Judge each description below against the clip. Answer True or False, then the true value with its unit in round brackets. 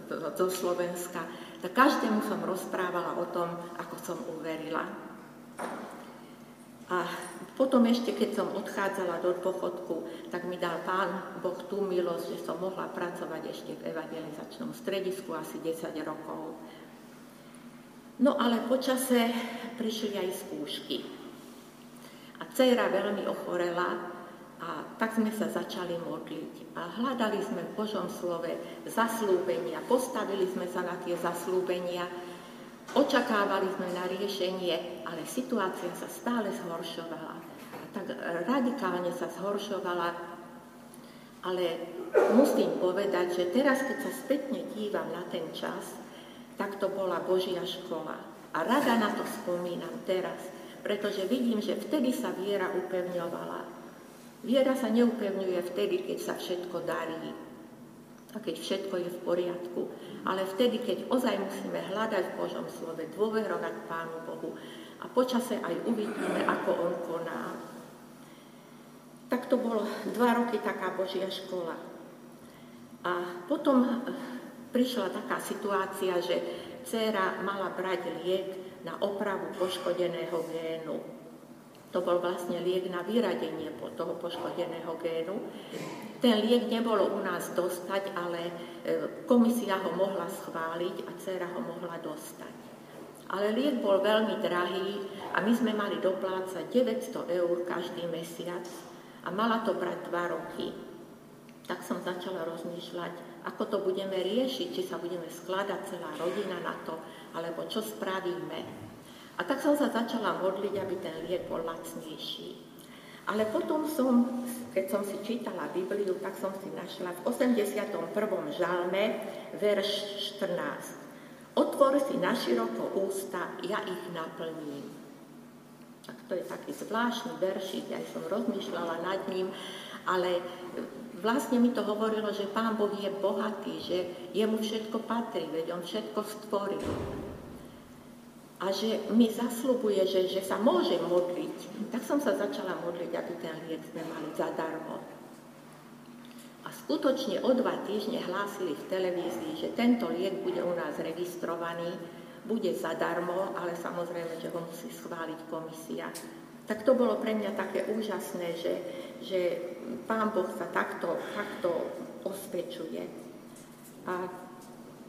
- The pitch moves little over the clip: False (3.7 semitones)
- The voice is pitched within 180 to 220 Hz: True (190 Hz)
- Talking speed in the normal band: True (130 wpm)